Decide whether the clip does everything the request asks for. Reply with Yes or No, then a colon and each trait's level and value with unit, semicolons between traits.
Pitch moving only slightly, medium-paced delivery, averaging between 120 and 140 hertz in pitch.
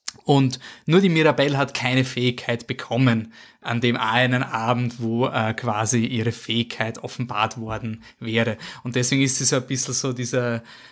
Yes: narrow, 2.2 semitones; average, 160 wpm; low, 125 Hz